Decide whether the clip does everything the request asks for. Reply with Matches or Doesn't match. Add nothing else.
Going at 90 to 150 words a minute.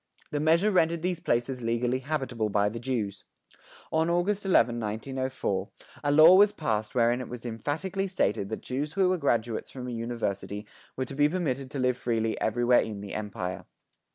Doesn't match